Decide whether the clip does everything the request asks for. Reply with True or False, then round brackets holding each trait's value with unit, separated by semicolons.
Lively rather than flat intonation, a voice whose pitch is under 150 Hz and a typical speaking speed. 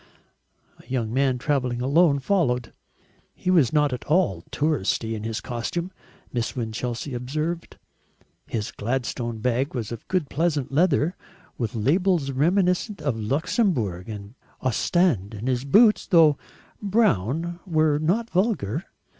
False (6.4 semitones; 140 Hz; 130 wpm)